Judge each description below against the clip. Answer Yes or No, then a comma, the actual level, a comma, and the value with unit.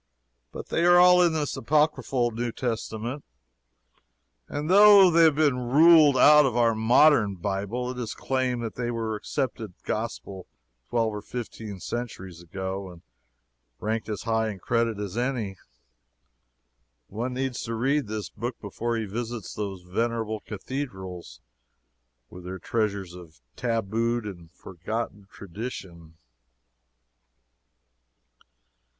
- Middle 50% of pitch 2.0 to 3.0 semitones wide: No, average, 4.1 semitones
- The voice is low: Yes, low, 115 Hz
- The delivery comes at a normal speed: No, slow, 125 wpm